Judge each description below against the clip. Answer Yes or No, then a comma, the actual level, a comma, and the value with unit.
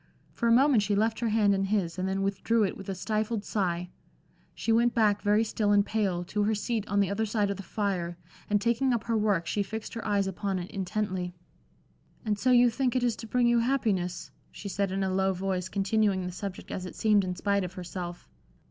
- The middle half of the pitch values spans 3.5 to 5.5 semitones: No, average, 2.7 semitones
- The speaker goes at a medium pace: No, fast, 230 wpm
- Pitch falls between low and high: No, high, 205 Hz